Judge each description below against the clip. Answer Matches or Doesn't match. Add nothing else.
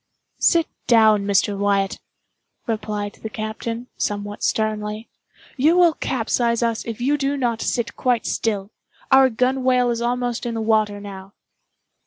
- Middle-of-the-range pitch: Doesn't match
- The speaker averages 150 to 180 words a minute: Doesn't match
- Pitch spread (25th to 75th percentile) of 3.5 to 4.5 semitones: Doesn't match